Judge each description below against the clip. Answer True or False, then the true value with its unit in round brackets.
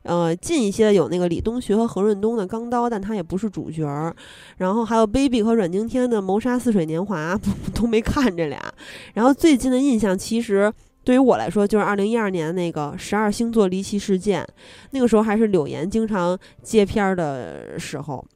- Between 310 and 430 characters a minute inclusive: True (315 characters per minute)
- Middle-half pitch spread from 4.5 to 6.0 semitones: False (4.0 semitones)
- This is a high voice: True (210 Hz)